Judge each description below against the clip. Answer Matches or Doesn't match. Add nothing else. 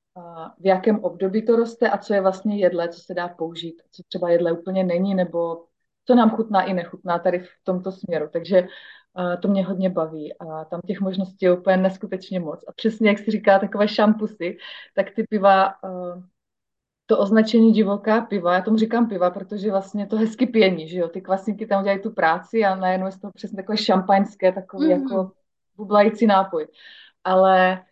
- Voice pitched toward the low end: Doesn't match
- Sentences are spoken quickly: Matches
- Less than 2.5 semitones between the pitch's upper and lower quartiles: Doesn't match